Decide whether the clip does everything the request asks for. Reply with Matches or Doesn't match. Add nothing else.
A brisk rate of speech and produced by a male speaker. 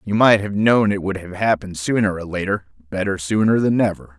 Matches